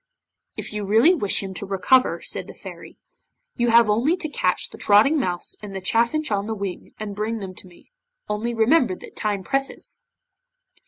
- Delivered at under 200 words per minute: Yes, average, 190 wpm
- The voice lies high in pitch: Yes, high, 215 Hz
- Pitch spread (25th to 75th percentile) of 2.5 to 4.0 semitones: Yes, average, 3.6 semitones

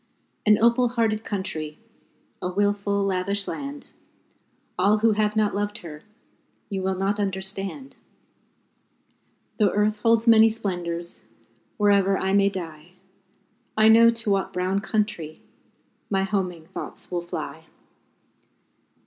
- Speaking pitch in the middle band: No, high, 200 Hz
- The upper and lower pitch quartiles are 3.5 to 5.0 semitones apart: No, narrow, 2.5 semitones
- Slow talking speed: Yes, slow, 120 wpm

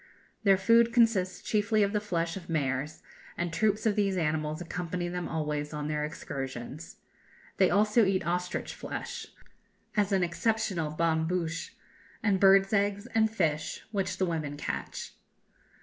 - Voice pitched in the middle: Yes, medium, 180 Hz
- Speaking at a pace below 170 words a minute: Yes, average, 150 wpm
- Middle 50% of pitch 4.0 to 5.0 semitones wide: Yes, average, 4.3 semitones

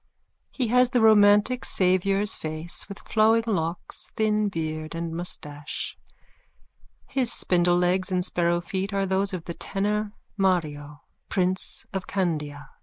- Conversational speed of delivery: No, slow, 125 wpm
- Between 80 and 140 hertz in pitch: No, medium, 185 Hz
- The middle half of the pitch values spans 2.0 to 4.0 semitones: Yes, average, 3.6 semitones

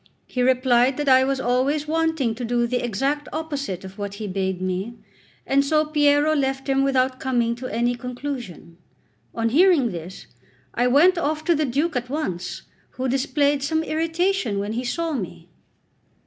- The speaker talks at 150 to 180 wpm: Yes, average, 170 wpm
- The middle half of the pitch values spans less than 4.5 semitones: Yes, average, 4.0 semitones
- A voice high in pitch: Yes, very high, 260 Hz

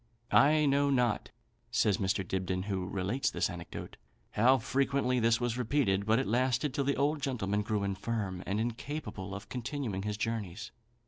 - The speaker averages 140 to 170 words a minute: Yes, average, 165 wpm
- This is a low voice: Yes, low, 115 Hz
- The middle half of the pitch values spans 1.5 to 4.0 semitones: No, average, 5.0 semitones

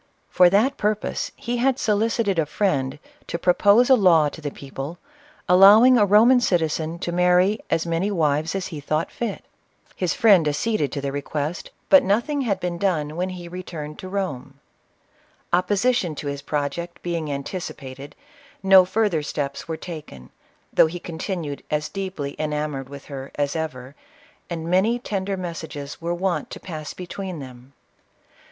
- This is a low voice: No, medium, 170 Hz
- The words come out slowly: No, average, 165 wpm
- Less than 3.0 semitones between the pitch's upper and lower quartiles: No, average, 4.8 semitones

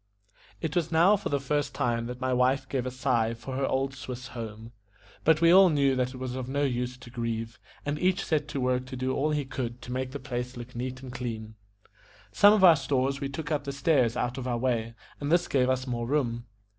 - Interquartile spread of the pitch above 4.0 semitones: No, narrow, 2.5 semitones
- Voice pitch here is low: Yes, low, 130 Hz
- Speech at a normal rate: No, fast, 240 wpm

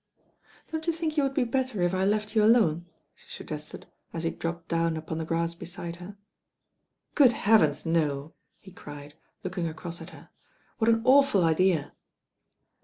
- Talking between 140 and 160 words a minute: No, average, 175 wpm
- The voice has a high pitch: No, medium, 175 Hz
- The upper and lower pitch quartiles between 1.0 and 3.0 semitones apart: No, wide, 5.5 semitones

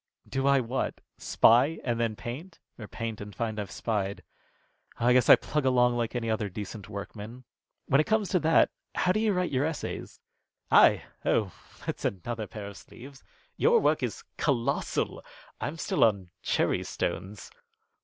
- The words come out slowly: No, average, 170 wpm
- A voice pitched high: No, low, 120 Hz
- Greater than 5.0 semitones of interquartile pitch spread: No, average, 4.7 semitones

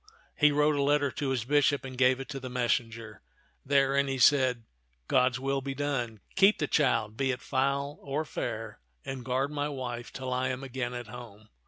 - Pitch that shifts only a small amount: Yes, narrow, 2.3 semitones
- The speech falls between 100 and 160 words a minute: No, average, 200 wpm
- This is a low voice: Yes, low, 130 Hz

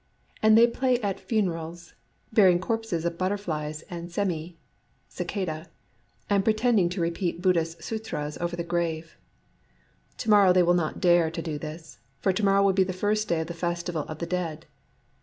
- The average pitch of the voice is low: No, medium, 175 Hz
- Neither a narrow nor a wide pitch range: Yes, average, 3.2 semitones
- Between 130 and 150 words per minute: No, average, 175 wpm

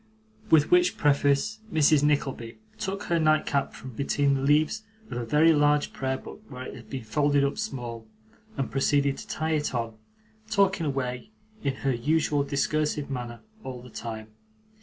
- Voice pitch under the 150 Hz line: Yes, medium, 140 Hz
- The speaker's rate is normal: Yes, average, 165 wpm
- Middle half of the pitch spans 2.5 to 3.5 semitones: Yes, average, 3.1 semitones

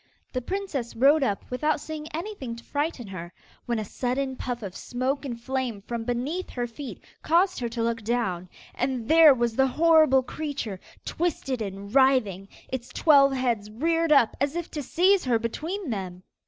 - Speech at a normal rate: Yes, average, 175 wpm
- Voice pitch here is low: No, very high, 255 Hz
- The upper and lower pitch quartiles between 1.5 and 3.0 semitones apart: No, average, 4.6 semitones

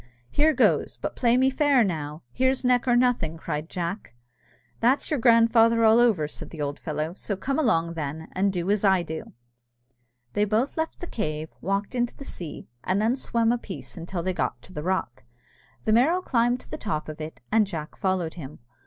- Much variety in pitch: Yes, wide, 6.7 semitones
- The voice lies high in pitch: Yes, high, 200 Hz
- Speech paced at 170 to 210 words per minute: Yes, average, 200 wpm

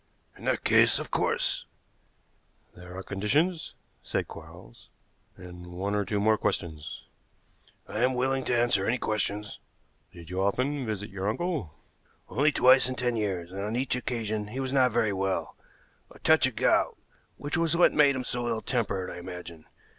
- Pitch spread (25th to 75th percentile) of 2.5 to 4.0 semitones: No, average, 5.0 semitones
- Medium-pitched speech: No, low, 110 Hz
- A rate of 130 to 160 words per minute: No, average, 175 wpm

